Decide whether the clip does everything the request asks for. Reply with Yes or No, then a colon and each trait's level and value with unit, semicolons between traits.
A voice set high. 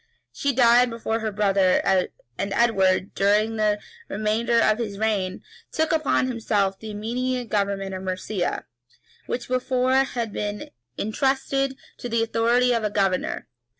Yes: high, 220 Hz